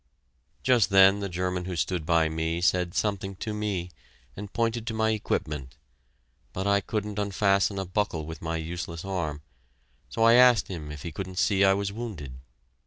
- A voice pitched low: Yes, very low, 95 Hz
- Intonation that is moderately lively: Yes, average, 3.7 semitones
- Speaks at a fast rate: No, average, 175 wpm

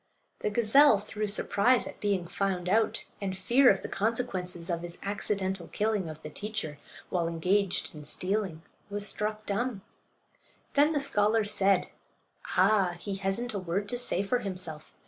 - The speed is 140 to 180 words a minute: Yes, average, 160 wpm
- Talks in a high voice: Yes, high, 200 Hz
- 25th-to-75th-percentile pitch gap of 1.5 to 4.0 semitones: Yes, average, 2.9 semitones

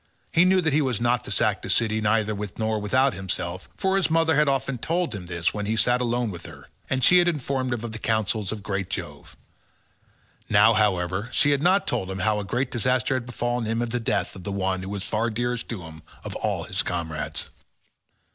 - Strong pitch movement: No, average, 4.3 semitones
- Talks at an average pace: No, fast, 230 wpm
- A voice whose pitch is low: Yes, low, 115 Hz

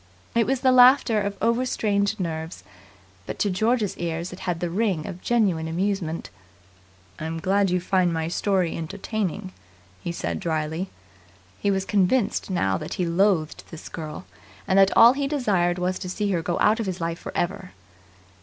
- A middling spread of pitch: Yes, average, 3.7 semitones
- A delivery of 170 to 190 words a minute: Yes, average, 175 wpm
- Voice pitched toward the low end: No, medium, 185 Hz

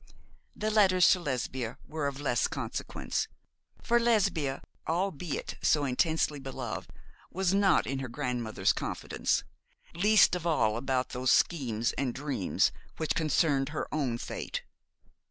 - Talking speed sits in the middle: No, slow, 130 wpm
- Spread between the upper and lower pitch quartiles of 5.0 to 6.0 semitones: Yes, wide, 5.5 semitones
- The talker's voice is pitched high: No, medium, 145 Hz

